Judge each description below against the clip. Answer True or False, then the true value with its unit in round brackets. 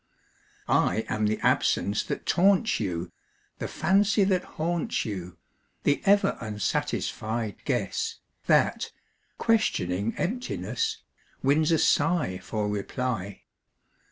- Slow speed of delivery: True (100 wpm)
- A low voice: True (125 Hz)